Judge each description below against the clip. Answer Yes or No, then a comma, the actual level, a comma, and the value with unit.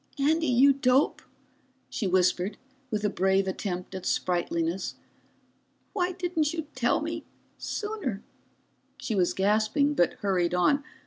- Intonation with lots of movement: Yes, wide, 7.9 semitones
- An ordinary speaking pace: No, slow, 125 wpm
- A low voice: No, high, 215 Hz